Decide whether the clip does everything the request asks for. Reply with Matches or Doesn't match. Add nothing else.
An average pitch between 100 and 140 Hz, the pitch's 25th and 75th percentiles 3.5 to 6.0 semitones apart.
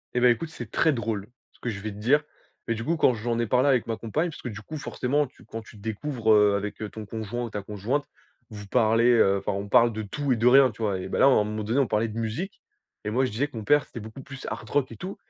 Matches